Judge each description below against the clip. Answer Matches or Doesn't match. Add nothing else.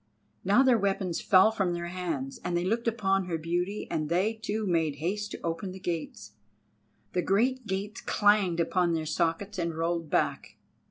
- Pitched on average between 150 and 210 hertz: Matches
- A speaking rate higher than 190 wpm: Doesn't match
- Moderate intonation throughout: Matches